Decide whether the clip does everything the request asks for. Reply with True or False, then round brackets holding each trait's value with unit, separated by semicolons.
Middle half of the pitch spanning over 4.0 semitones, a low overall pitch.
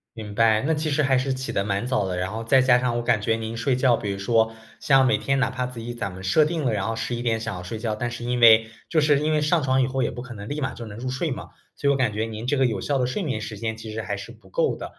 False (3.3 semitones; 120 Hz)